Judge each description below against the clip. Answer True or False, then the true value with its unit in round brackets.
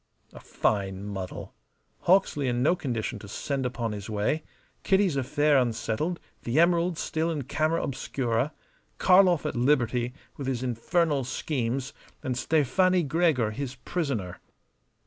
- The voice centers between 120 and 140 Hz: True (135 Hz)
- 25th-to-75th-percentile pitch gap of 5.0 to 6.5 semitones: True (5.3 semitones)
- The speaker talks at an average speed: False (130 wpm)